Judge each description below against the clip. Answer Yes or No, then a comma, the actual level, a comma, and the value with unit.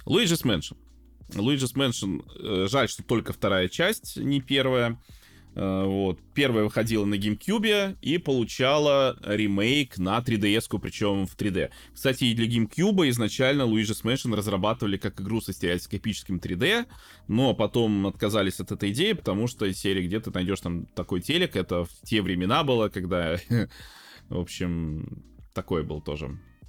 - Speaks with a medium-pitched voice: No, low, 105 Hz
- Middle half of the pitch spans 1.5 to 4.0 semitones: No, average, 4.6 semitones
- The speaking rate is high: No, average, 140 wpm